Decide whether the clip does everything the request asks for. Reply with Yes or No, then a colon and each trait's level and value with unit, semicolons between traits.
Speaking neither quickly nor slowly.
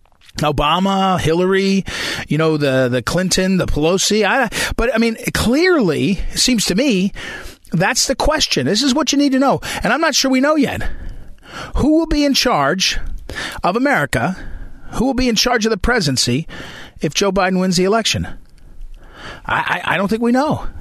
Yes: average, 180 wpm